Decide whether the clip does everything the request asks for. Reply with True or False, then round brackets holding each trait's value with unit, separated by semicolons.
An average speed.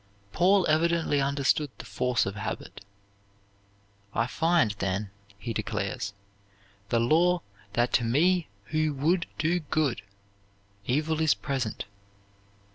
False (115 wpm)